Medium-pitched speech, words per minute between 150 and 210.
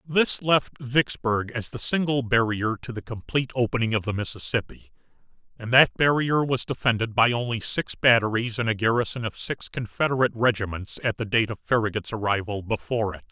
No: low, 115 Hz; average, 170 wpm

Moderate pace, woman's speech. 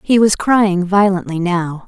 Yes: average, 160 wpm; female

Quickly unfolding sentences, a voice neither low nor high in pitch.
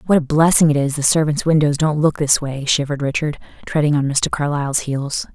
Yes: fast, 215 wpm; medium, 145 Hz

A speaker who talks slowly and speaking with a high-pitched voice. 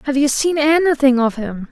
No: fast, 210 wpm; very high, 275 Hz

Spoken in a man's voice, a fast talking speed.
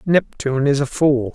No: male; average, 180 wpm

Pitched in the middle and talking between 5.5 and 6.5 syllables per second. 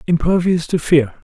No: medium, 165 Hz; 4.6 syllables/s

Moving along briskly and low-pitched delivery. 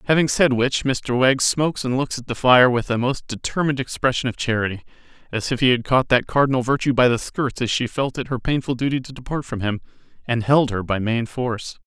Yes: fast, 235 wpm; low, 125 Hz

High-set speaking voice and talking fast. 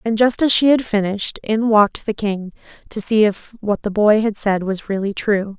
Yes: high, 210 Hz; fast, 225 wpm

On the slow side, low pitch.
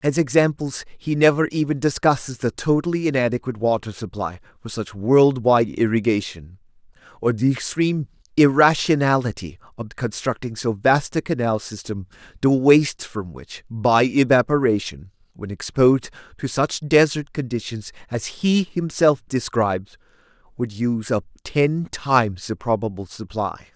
Yes: slow, 125 wpm; low, 120 Hz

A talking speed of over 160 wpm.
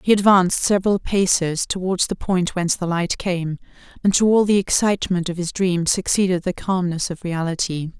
Yes: average, 180 wpm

